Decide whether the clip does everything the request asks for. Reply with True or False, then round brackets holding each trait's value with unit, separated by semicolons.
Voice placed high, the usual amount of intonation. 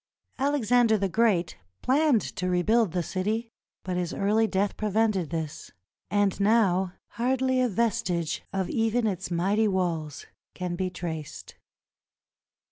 True (200 Hz; 4.1 semitones)